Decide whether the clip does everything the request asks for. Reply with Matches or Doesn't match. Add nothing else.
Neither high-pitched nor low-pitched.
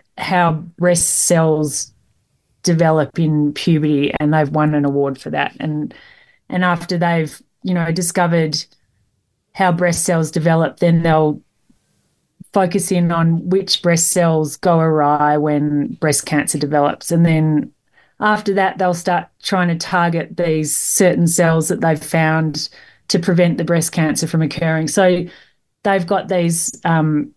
Matches